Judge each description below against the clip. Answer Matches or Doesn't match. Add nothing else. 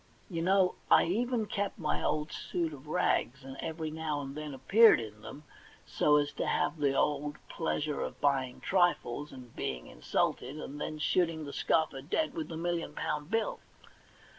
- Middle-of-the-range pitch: Matches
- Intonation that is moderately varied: Matches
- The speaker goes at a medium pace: Matches